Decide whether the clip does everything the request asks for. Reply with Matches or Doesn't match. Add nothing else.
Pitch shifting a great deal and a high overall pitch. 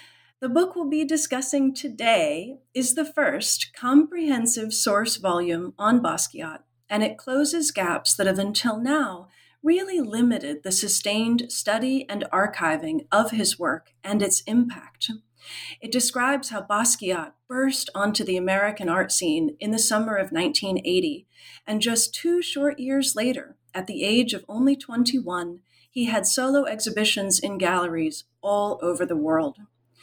Matches